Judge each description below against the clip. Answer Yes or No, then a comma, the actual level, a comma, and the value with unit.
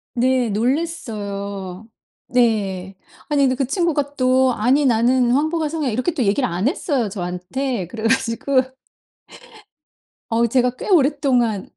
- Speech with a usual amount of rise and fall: Yes, average, 4.5 semitones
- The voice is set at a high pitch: Yes, very high, 250 Hz